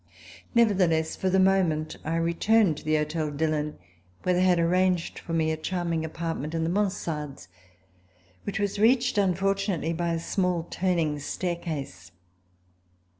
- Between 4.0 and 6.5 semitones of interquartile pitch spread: No, average, 3.1 semitones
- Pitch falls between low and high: Yes, medium, 170 Hz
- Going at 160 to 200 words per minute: No, average, 140 wpm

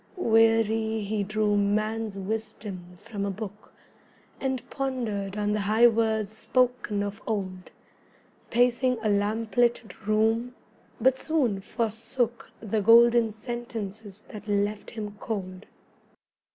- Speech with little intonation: Yes, narrow, 2.3 semitones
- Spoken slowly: Yes, slow, 110 wpm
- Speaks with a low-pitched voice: No, high, 220 Hz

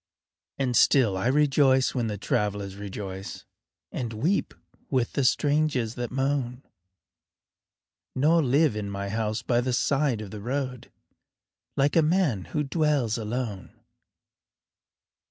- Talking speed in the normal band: No, slow, 125 wpm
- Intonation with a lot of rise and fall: No, average, 4.9 semitones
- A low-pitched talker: Yes, low, 125 Hz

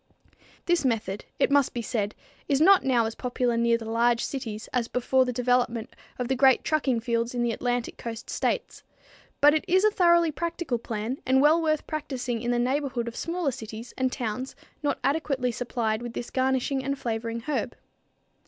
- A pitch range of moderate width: Yes, average, 3.3 semitones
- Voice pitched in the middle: No, very high, 250 Hz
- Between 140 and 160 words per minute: No, average, 185 wpm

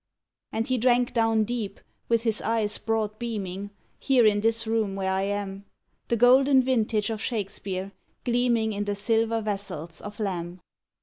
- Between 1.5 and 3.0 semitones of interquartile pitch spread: Yes, narrow, 2.5 semitones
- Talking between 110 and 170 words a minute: Yes, average, 160 wpm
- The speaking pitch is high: Yes, high, 220 Hz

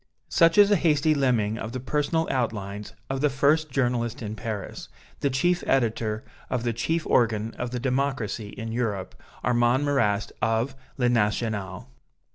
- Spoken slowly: No, average, 155 wpm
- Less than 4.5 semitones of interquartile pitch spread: Yes, average, 4.0 semitones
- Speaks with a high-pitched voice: No, low, 120 Hz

